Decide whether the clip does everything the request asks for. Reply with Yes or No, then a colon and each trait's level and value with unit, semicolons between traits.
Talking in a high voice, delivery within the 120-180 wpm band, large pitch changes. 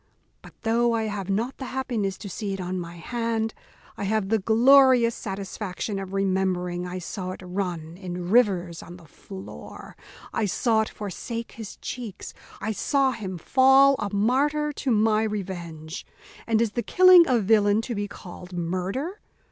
No: high, 205 Hz; average, 165 wpm; average, 4.1 semitones